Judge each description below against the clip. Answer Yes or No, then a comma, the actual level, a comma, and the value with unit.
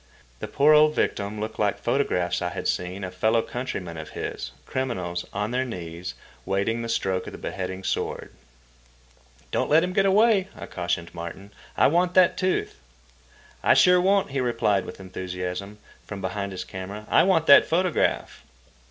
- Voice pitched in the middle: No, low, 105 Hz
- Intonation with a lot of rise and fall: Yes, wide, 8.5 semitones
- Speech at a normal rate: Yes, average, 170 wpm